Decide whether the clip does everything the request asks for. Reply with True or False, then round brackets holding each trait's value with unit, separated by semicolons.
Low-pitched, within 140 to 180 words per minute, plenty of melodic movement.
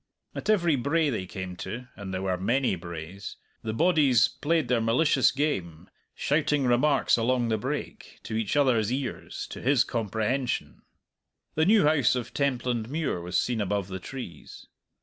True (120 Hz; 155 wpm; 5.8 semitones)